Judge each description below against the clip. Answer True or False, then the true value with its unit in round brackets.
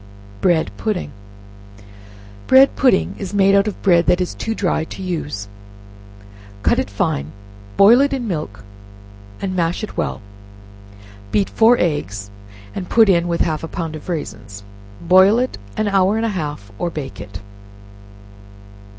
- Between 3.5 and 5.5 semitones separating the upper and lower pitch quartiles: True (5.0 semitones)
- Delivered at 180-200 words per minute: False (150 wpm)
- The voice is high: False (180 Hz)